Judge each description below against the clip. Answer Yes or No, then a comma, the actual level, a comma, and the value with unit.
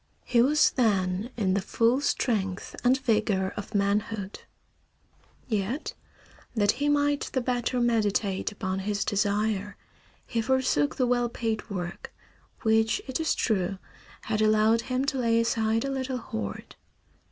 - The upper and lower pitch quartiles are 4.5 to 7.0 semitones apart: No, average, 3.5 semitones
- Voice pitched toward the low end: No, high, 220 Hz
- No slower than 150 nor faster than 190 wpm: No, average, 140 wpm